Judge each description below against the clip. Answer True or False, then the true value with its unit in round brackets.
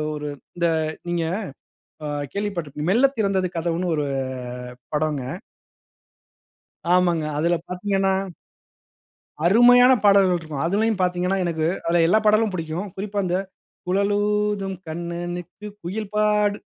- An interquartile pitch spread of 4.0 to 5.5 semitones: False (3.3 semitones)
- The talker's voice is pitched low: False (185 Hz)